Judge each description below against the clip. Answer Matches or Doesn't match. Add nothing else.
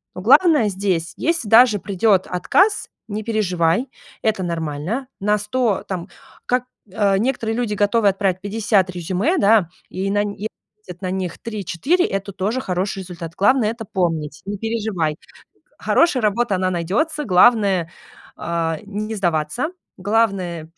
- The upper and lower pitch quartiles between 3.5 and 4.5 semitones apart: Matches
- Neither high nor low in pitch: Doesn't match